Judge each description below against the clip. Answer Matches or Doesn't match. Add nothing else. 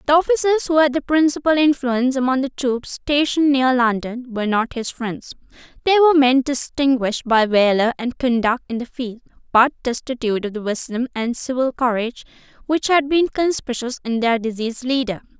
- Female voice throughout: Matches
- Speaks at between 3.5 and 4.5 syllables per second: Doesn't match